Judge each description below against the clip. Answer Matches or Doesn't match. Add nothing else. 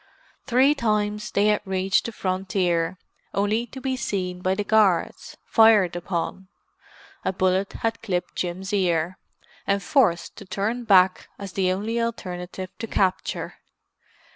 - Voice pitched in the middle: Doesn't match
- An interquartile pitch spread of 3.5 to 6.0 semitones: Doesn't match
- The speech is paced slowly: Matches